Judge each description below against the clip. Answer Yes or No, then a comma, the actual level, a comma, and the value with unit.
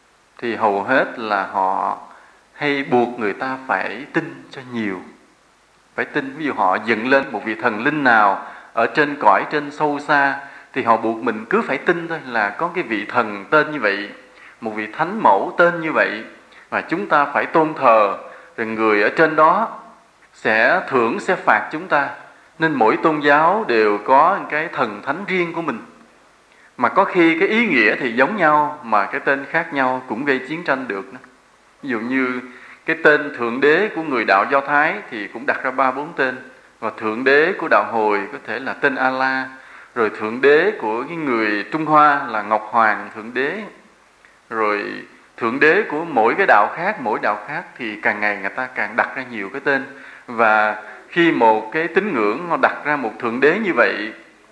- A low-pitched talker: Yes, low, 130 Hz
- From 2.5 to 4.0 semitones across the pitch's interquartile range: No, average, 5.2 semitones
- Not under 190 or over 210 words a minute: Yes, average, 200 wpm